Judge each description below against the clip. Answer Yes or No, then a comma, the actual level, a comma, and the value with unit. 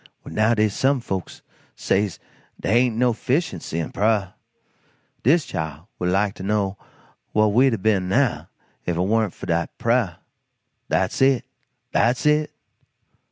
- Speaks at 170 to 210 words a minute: No, average, 150 wpm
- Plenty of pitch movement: No, average, 4.6 semitones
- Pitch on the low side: Yes, low, 110 Hz